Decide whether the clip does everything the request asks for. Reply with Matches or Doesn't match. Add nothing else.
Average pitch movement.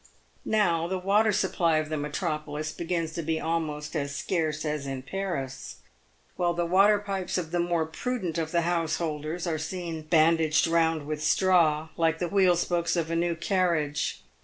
Doesn't match